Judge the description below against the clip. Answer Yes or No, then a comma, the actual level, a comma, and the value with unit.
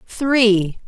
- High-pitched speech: Yes, high, 220 Hz